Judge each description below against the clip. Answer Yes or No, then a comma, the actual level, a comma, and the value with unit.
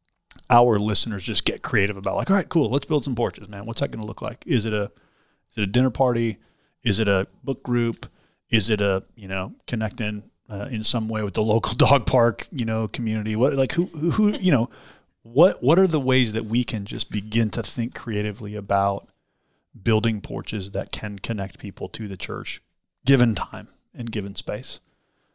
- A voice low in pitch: Yes, low, 110 Hz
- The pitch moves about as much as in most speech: Yes, average, 3.2 semitones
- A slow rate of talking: No, fast, 205 wpm